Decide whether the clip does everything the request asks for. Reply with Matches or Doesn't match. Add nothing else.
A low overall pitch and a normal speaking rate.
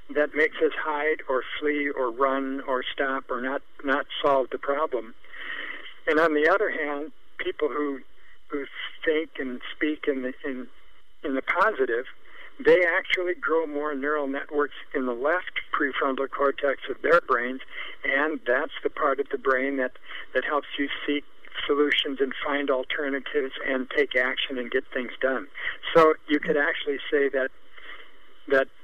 Doesn't match